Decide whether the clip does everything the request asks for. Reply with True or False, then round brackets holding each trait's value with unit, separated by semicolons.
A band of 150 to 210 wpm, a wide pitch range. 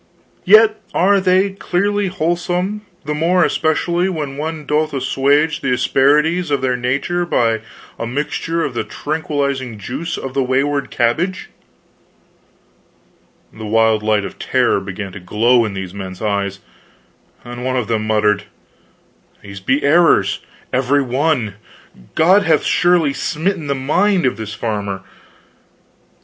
False (135 wpm; 6.9 semitones)